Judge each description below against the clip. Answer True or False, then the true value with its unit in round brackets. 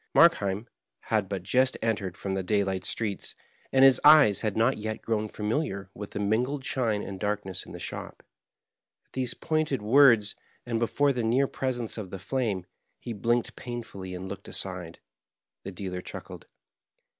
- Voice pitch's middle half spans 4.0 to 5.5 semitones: True (4.3 semitones)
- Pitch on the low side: True (110 Hz)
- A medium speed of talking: True (165 wpm)